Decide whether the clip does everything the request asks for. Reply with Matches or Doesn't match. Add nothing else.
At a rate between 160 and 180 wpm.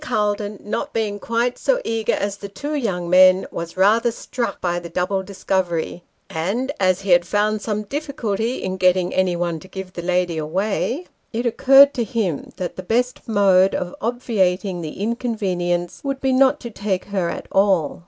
Matches